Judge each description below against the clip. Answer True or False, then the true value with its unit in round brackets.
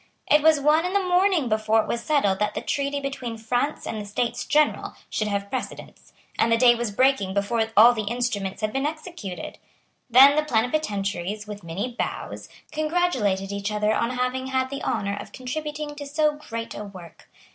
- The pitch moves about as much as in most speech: False (5.8 semitones)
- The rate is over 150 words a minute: True (190 wpm)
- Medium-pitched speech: False (245 Hz)